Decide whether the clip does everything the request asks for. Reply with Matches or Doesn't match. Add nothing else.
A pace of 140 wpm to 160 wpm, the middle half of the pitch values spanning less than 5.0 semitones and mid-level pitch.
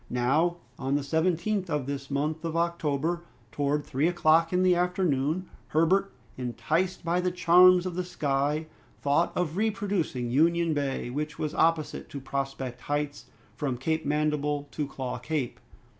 Matches